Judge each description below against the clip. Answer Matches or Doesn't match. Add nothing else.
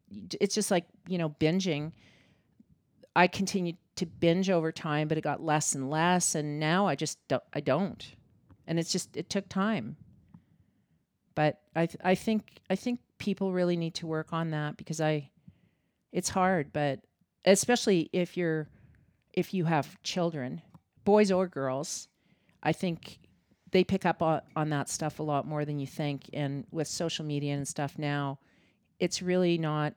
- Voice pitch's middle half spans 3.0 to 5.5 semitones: Matches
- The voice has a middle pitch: Matches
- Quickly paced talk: Doesn't match